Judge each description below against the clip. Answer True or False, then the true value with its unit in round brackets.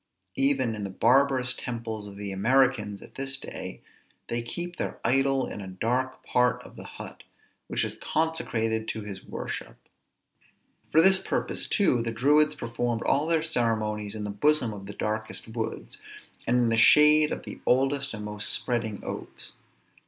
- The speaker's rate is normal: True (165 wpm)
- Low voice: True (120 Hz)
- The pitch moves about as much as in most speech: True (4.2 semitones)